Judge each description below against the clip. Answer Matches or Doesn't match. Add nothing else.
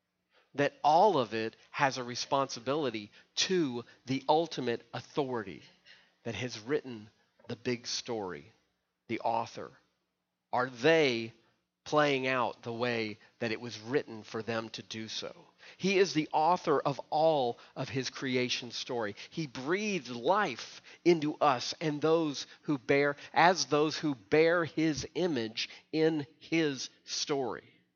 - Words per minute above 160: Doesn't match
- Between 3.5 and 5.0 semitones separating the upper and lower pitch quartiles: Matches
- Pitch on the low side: Matches